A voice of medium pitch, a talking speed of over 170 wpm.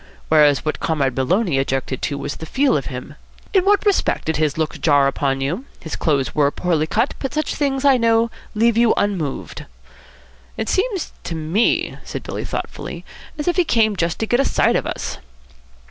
Yes: medium, 180 Hz; average, 190 wpm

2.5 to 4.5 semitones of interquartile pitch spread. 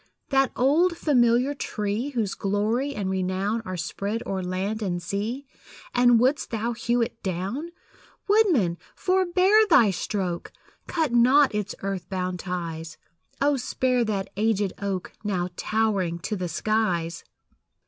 No: average, 5.3 semitones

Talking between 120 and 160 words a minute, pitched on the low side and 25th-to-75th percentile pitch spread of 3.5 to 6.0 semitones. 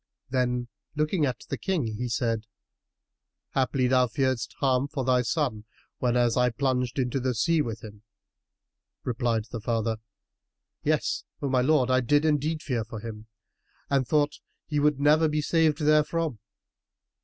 Yes: average, 150 wpm; low, 130 Hz; average, 3.9 semitones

